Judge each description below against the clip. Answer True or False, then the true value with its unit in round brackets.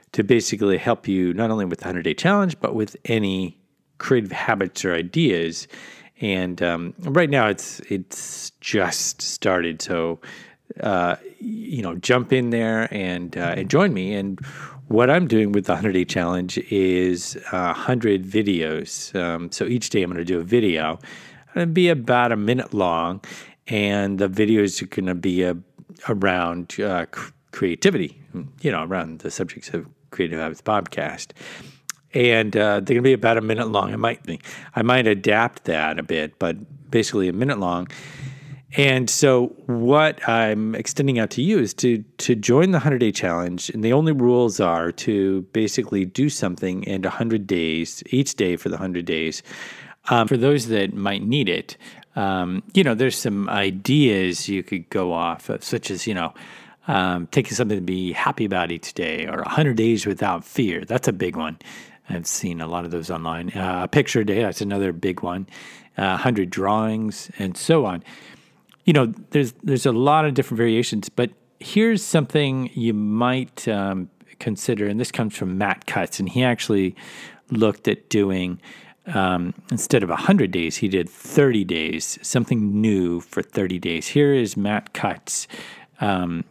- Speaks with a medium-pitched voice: False (105 Hz)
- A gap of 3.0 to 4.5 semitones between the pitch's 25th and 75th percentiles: False (5.2 semitones)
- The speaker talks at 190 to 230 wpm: False (175 wpm)